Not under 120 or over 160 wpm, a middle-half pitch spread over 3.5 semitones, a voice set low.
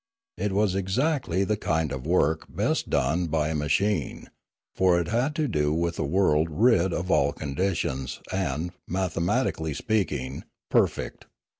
Yes: average, 150 wpm; average, 4.5 semitones; very low, 85 Hz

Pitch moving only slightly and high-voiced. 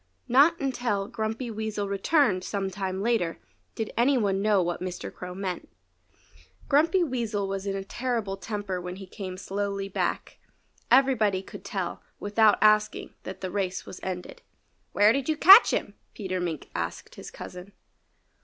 No: average, 3.8 semitones; high, 205 Hz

